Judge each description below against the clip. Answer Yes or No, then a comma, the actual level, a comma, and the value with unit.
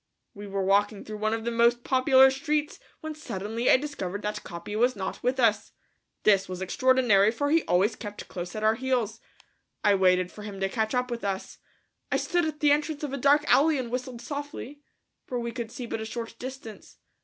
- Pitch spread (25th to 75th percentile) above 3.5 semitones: Yes, average, 4.4 semitones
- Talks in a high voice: Yes, high, 235 Hz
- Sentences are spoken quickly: Yes, fast, 210 wpm